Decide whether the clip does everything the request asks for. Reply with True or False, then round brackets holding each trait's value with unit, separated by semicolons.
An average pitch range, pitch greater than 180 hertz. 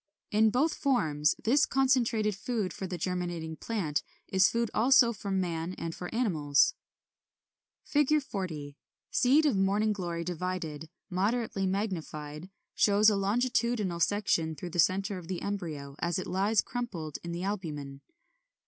True (4.8 semitones; 190 Hz)